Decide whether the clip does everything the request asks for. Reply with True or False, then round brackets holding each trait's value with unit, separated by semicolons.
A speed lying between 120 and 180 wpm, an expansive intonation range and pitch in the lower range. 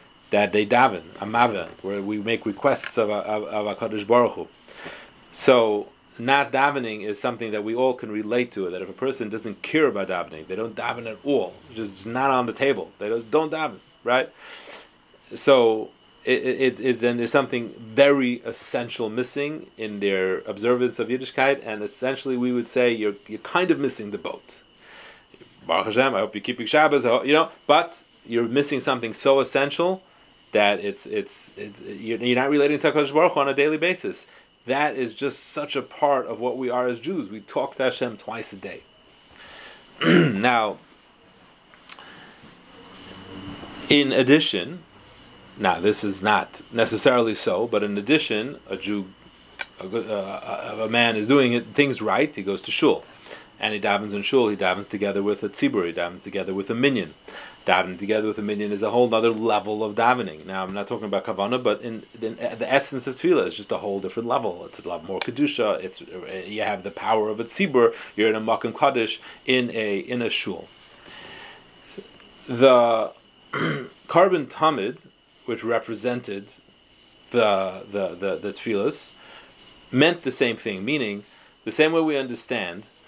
False (175 wpm; 4.5 semitones; 115 Hz)